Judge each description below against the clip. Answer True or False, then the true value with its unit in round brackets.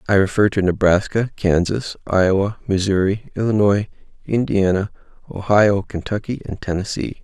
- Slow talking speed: True (110 wpm)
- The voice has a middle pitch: False (100 Hz)